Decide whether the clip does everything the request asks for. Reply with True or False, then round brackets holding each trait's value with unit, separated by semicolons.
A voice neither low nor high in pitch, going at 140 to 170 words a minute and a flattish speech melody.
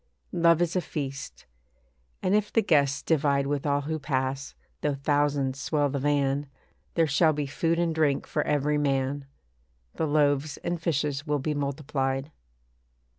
True (145 Hz; 155 wpm; 2.2 semitones)